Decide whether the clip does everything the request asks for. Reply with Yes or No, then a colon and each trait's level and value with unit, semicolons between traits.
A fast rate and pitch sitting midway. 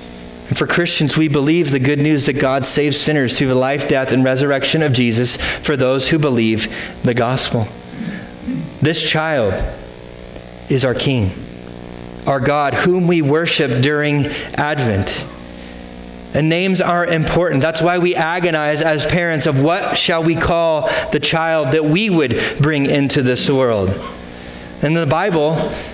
No: average, 150 wpm; medium, 145 Hz